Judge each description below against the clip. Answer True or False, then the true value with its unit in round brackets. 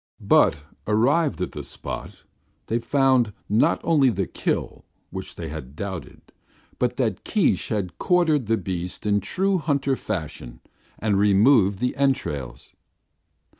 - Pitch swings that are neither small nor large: False (6.4 semitones)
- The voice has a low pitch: True (110 Hz)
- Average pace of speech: False (130 wpm)